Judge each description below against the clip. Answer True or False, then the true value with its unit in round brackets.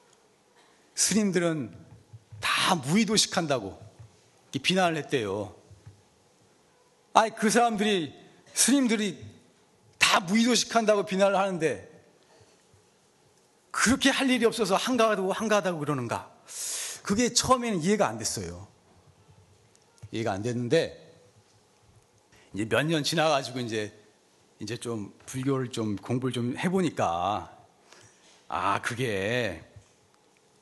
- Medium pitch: True (165 Hz)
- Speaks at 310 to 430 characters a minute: False (225 characters per minute)